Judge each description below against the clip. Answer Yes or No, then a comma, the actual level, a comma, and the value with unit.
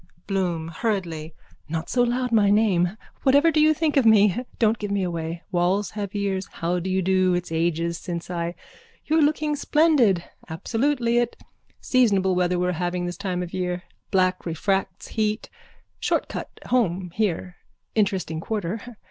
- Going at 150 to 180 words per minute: Yes, average, 160 wpm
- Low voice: No, high, 190 Hz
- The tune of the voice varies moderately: Yes, average, 4.3 semitones